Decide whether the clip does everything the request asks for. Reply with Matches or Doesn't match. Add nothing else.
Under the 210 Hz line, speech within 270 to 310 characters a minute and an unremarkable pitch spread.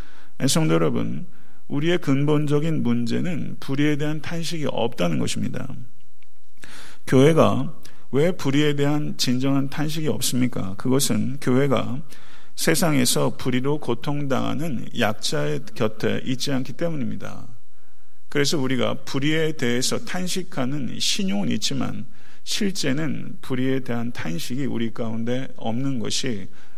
Matches